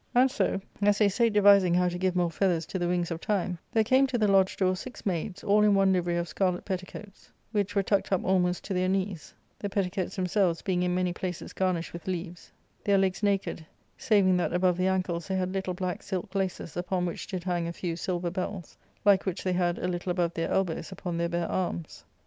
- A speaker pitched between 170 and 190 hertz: Yes, medium, 185 Hz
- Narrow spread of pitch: Yes, narrow, 1.9 semitones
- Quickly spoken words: Yes, fast, 225 wpm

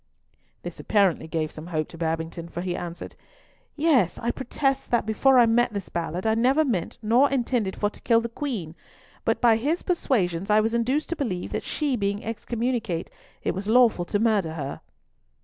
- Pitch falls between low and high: No, high, 220 Hz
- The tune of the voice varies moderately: No, wide, 6.1 semitones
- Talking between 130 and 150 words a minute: No, average, 185 wpm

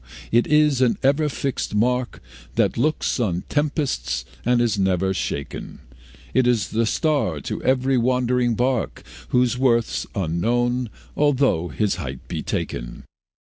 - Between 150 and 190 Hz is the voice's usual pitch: No, low, 120 Hz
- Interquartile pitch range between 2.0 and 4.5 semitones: No, average, 5.3 semitones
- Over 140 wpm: No, slow, 135 wpm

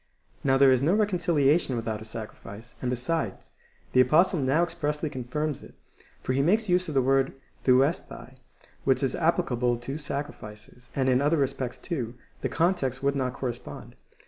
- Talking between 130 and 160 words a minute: No, average, 170 wpm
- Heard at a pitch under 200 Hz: Yes, low, 135 Hz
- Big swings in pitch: No, average, 3.8 semitones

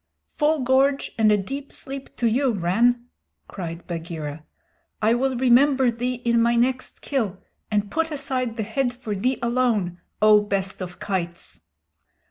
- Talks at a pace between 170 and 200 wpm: No, average, 150 wpm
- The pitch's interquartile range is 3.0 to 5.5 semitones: Yes, average, 4.8 semitones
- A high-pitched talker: Yes, high, 235 Hz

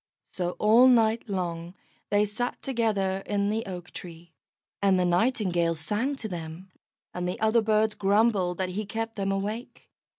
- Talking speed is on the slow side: No, average, 160 wpm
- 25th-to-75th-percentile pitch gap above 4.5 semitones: No, average, 3.7 semitones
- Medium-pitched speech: No, high, 200 Hz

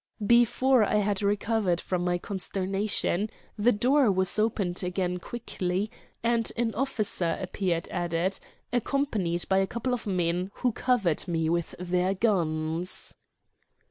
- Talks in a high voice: Yes, high, 195 Hz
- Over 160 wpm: No, slow, 135 wpm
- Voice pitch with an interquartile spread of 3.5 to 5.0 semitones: Yes, average, 4.1 semitones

